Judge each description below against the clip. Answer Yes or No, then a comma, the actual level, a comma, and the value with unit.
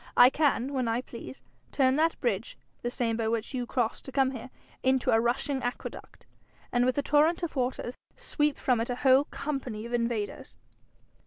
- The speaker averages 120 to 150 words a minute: No, average, 185 wpm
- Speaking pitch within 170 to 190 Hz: No, very high, 250 Hz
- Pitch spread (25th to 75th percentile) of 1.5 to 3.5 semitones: Yes, narrow, 2.4 semitones